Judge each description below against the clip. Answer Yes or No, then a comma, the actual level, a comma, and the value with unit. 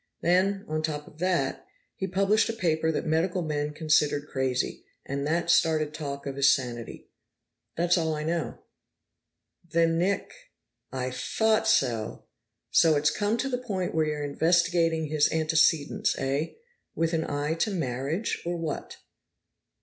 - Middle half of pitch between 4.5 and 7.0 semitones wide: No, average, 3.0 semitones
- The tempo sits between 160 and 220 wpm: No, average, 150 wpm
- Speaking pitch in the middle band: Yes, medium, 160 Hz